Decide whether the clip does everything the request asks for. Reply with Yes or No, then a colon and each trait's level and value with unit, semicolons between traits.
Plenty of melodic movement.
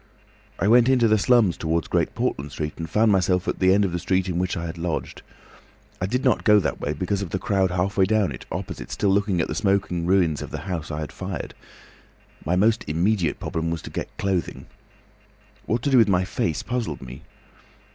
No: average, 3.6 semitones